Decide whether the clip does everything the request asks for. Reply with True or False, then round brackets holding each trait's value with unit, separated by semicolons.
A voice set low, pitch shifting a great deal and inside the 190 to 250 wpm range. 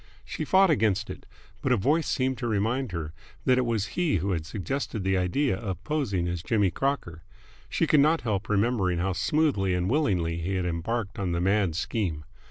True (100 Hz; 6.2 semitones; 195 wpm)